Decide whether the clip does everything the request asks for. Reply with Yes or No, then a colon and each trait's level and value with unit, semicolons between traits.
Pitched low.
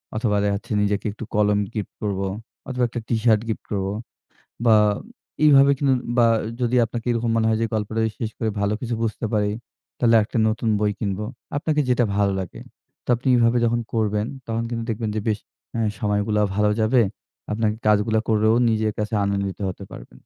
Yes: low, 110 Hz